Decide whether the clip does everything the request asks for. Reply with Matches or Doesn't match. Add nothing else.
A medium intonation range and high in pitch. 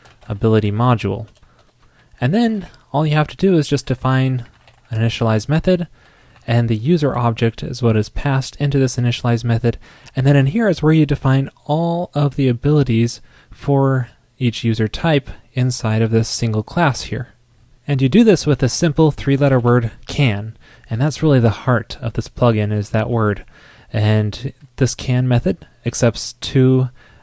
Doesn't match